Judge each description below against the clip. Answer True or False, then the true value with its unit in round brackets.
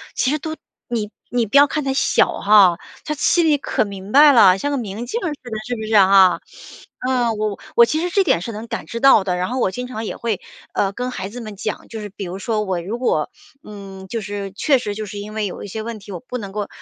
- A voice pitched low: False (215 Hz)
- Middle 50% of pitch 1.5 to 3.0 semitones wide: False (4.0 semitones)